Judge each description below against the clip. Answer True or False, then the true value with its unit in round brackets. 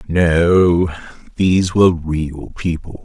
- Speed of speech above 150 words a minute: False (100 wpm)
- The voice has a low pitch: True (85 Hz)